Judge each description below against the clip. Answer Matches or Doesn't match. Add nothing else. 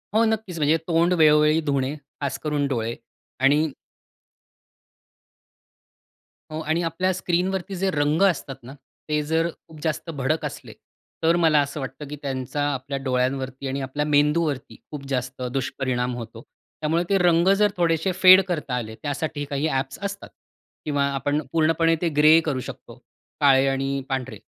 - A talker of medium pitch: Matches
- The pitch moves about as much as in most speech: Matches